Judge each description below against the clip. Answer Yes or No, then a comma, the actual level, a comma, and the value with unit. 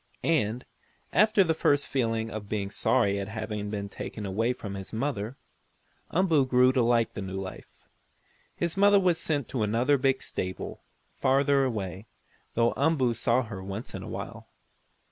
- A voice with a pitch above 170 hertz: No, low, 115 Hz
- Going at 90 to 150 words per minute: No, average, 165 wpm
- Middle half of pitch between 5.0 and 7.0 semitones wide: Yes, average, 5.3 semitones